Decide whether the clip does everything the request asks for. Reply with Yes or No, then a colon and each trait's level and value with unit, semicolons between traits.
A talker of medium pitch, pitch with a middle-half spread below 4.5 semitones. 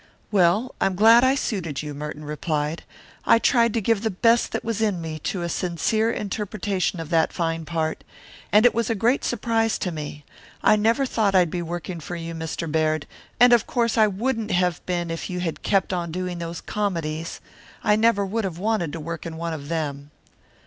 No: medium, 180 Hz; average, 5.1 semitones